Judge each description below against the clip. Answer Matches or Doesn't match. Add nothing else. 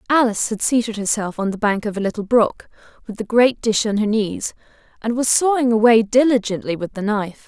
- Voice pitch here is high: Matches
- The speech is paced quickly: Matches